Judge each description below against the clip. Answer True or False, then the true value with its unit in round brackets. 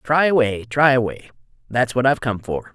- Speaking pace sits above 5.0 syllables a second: True (5.3 syllables/s)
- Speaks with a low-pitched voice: True (125 Hz)